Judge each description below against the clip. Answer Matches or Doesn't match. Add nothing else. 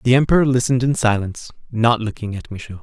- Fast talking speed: Doesn't match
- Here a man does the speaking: Matches